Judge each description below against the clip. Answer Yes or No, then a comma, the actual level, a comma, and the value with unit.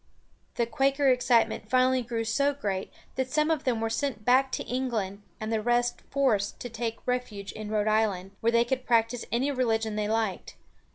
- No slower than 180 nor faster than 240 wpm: Yes, average, 185 wpm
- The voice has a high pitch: Yes, high, 235 Hz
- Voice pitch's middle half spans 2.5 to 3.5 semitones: Yes, average, 2.9 semitones